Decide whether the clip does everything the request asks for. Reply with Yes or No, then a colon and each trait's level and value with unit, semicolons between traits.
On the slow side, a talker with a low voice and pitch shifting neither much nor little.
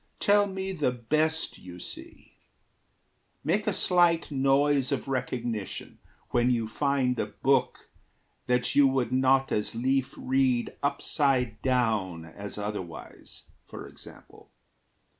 Yes: slow, 120 wpm; low, 130 Hz; average, 3.6 semitones